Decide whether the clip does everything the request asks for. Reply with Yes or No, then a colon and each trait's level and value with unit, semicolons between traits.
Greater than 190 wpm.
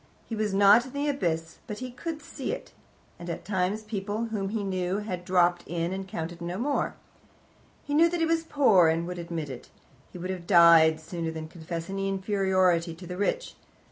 Yes: fast, 205 wpm